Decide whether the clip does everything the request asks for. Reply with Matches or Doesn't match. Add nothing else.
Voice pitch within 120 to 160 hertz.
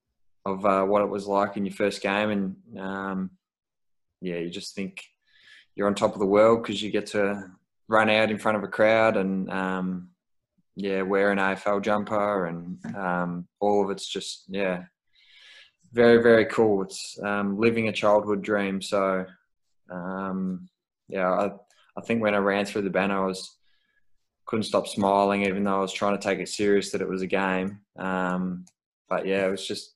Doesn't match